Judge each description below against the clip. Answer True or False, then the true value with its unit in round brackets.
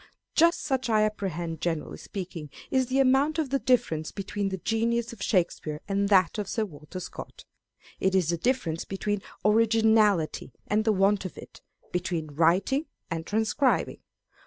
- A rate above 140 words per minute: True (160 wpm)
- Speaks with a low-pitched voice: False (205 Hz)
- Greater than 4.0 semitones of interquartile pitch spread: True (5.0 semitones)